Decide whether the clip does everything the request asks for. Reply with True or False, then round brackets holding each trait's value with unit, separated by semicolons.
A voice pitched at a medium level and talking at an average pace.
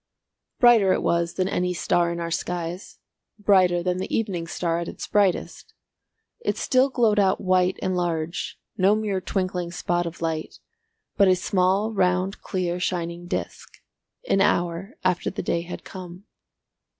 True (180 Hz; 155 wpm)